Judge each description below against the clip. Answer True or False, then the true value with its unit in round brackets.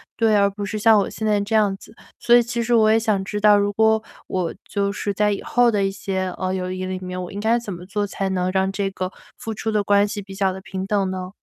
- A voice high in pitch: True (200 Hz)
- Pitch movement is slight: True (2.1 semitones)